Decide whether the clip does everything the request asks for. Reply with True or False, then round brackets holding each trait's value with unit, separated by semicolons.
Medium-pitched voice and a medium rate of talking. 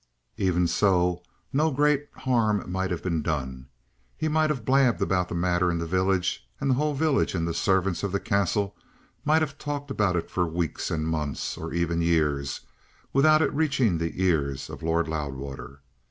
False (90 Hz; 185 wpm)